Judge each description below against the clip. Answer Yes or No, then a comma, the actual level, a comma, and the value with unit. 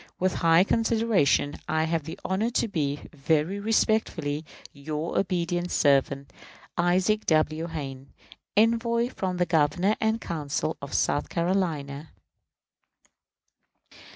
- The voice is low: No, medium, 170 Hz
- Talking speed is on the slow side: Yes, slow, 110 wpm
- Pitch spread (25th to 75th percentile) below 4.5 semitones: No, average, 4.9 semitones